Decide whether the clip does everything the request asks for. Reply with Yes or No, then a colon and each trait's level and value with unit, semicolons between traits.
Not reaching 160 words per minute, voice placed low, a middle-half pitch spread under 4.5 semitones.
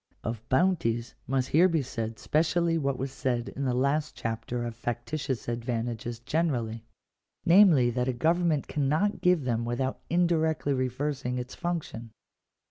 No: average, 140 wpm; low, 130 Hz; average, 5.0 semitones